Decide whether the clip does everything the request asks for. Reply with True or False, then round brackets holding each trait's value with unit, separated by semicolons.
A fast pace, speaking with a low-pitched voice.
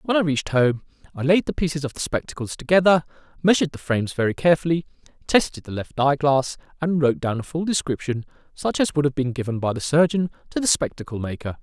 False (210 wpm; 145 Hz)